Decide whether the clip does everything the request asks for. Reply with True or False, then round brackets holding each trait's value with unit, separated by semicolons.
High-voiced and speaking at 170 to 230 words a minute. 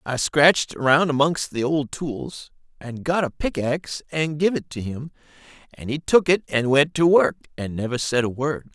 False (145 Hz; 200 wpm)